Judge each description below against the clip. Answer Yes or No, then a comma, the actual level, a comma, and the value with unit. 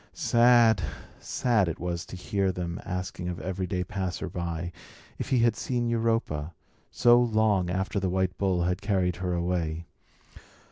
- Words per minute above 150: No, average, 145 wpm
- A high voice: No, very low, 95 Hz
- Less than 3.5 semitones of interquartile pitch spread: No, average, 3.8 semitones